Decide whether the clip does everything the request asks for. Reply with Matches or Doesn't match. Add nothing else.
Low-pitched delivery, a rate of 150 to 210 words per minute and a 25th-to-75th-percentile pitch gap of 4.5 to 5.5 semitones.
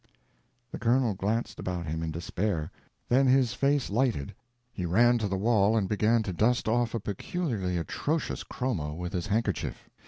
Matches